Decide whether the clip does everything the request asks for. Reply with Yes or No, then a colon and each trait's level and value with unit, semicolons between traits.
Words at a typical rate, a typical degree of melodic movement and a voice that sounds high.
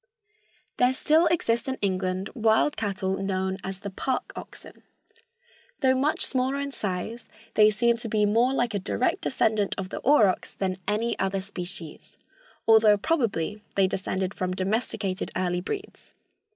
Yes: average, 150 wpm; average, 4.2 semitones; high, 210 Hz